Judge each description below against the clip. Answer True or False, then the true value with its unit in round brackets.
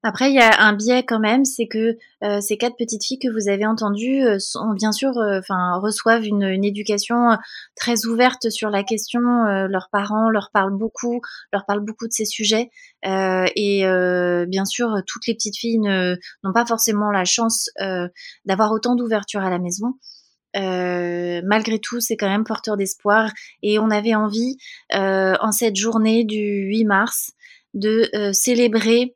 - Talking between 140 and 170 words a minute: False (185 wpm)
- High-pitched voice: True (215 Hz)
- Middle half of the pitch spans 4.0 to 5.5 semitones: False (2.7 semitones)